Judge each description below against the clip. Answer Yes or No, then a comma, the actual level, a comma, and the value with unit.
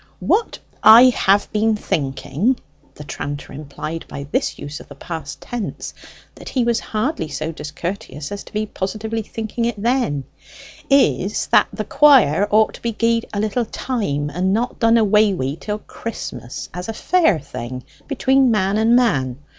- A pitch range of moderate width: No, wide, 7.3 semitones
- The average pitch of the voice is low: No, high, 210 Hz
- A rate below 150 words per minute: No, average, 165 wpm